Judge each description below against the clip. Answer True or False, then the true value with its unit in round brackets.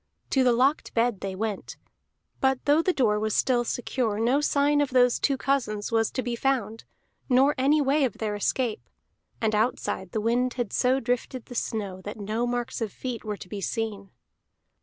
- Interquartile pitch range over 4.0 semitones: False (3.5 semitones)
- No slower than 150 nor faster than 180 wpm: False (190 wpm)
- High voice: True (240 Hz)